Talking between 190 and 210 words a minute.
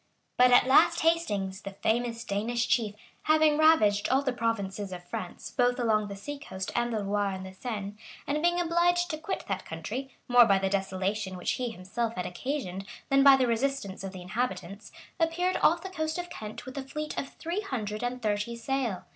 Yes: average, 200 wpm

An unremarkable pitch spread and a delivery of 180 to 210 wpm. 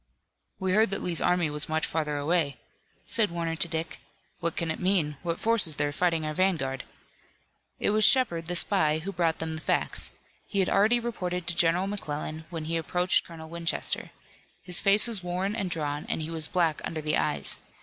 Yes: average, 3.0 semitones; average, 200 wpm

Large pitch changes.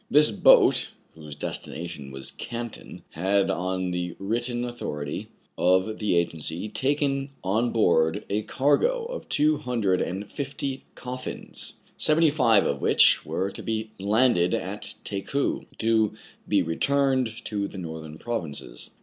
Yes: wide, 6.5 semitones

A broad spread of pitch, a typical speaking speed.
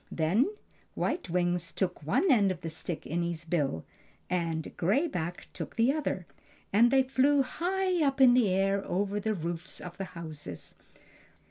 Yes: wide, 7.3 semitones; average, 165 wpm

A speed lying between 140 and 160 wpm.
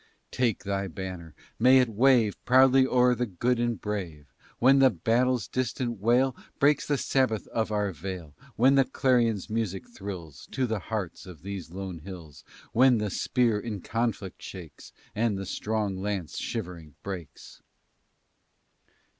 Yes: average, 145 wpm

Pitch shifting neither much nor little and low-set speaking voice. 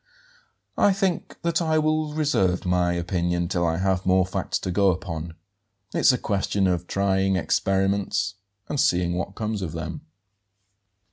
Yes: average, 3.5 semitones; very low, 95 Hz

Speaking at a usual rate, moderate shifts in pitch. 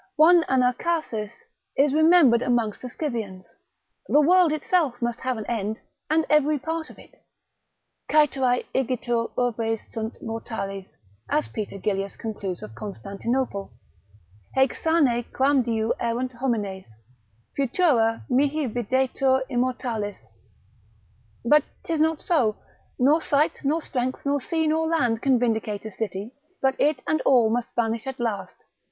No: slow, 130 wpm; average, 4.6 semitones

